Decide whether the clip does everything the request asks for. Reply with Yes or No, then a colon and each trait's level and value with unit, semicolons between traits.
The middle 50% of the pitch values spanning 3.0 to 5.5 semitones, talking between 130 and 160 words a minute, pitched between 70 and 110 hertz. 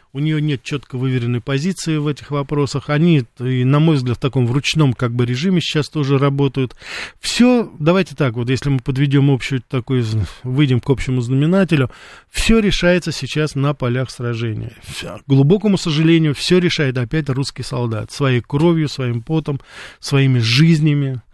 No: average, 3.3 semitones; average, 155 wpm; medium, 140 Hz